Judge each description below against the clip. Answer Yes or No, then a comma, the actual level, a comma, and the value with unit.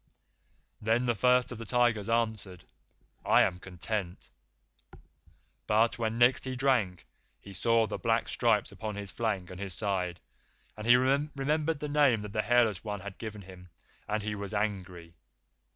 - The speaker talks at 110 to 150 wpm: No, average, 160 wpm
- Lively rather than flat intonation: No, average, 3.7 semitones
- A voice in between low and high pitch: No, low, 110 Hz